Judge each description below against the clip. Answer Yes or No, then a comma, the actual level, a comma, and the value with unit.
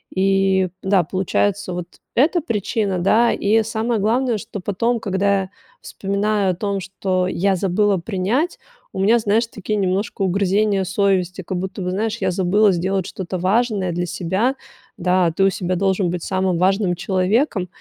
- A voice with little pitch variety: Yes, narrow, 2.3 semitones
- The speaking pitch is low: No, high, 195 Hz